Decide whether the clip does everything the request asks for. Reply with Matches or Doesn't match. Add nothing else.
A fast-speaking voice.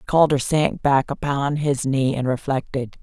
Doesn't match